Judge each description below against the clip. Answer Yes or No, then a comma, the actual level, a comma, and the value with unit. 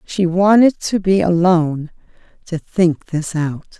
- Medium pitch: Yes, medium, 175 Hz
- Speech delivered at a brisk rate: No, average, 140 wpm